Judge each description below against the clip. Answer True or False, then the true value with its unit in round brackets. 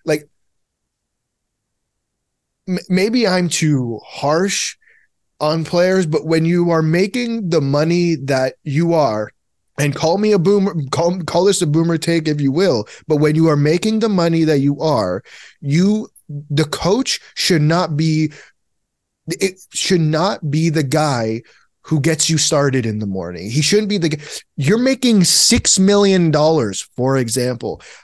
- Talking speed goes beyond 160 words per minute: False (150 wpm)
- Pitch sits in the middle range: True (160 Hz)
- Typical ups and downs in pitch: True (3.6 semitones)